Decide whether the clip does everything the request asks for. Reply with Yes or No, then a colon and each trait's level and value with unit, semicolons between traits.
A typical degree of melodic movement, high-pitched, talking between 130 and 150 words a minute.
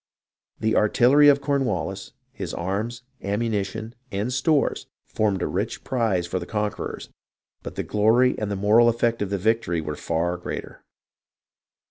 No: average, 3.4 semitones; low, 110 Hz; average, 145 wpm